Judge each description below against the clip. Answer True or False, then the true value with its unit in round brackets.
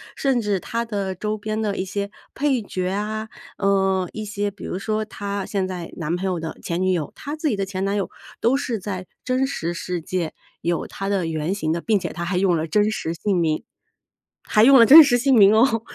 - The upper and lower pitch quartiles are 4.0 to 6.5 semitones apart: False (3.1 semitones)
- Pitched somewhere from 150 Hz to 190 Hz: False (200 Hz)